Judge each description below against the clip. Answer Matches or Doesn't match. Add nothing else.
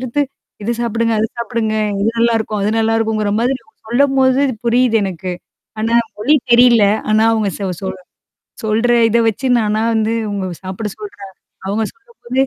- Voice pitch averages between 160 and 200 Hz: Doesn't match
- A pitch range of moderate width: Doesn't match